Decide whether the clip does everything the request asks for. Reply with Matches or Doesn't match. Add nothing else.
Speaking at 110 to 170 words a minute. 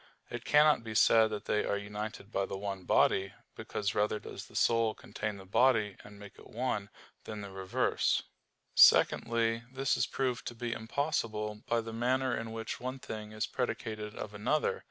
Doesn't match